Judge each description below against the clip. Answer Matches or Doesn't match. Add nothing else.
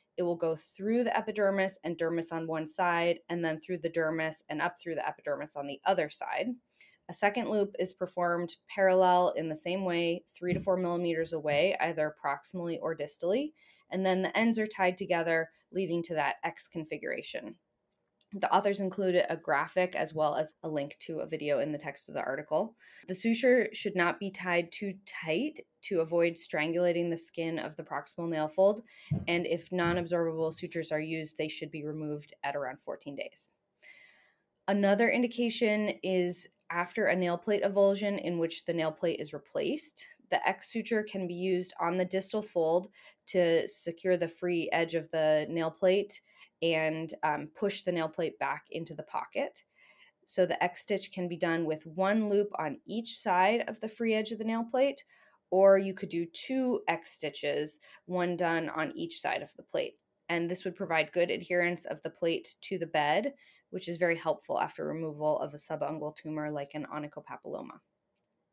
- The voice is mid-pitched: Matches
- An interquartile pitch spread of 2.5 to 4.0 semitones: Matches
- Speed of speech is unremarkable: Matches